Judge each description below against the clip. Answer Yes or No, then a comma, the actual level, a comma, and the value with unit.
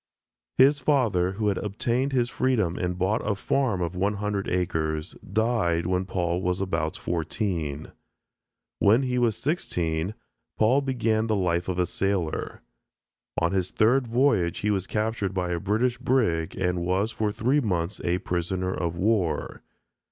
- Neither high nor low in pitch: No, very low, 95 Hz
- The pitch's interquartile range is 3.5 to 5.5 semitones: Yes, average, 4.4 semitones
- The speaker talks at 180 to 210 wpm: No, average, 155 wpm